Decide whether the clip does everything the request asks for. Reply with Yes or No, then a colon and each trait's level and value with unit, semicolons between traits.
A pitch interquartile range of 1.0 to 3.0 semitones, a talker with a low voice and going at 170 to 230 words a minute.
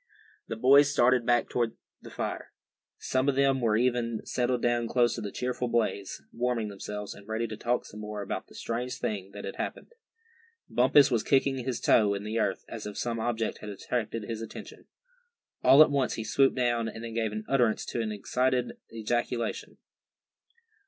Yes: narrow, 2.4 semitones; low, 120 Hz; average, 185 wpm